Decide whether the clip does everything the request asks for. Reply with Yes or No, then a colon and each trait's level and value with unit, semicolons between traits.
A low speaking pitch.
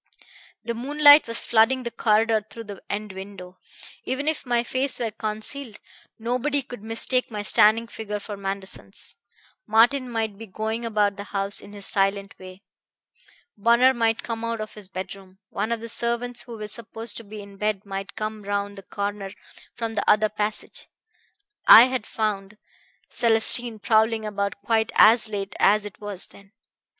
No: high, 215 Hz